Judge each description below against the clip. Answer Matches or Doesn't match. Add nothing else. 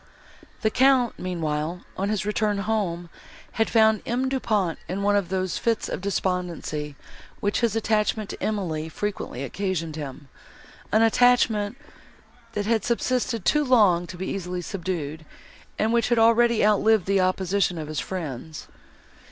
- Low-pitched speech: Doesn't match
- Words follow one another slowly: Doesn't match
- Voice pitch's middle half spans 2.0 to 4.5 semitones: Matches